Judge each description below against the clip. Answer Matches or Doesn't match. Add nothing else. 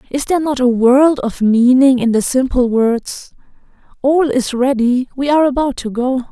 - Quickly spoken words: Doesn't match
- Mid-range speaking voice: Doesn't match